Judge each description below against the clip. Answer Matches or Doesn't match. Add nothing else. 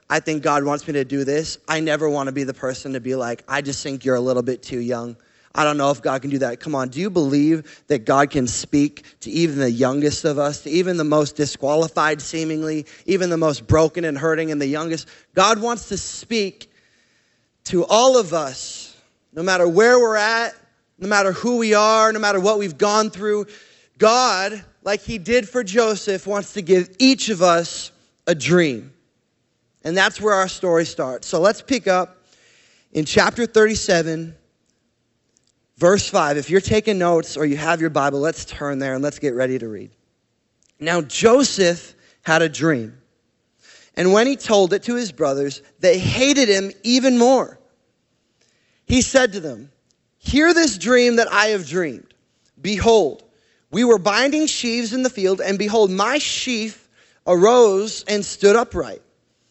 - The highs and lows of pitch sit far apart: Matches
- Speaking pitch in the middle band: Matches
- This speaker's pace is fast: Doesn't match